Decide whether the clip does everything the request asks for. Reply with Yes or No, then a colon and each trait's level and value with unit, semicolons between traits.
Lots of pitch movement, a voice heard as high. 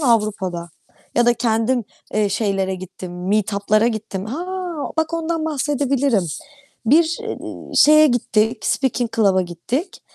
Yes: wide, 5.9 semitones; high, 225 Hz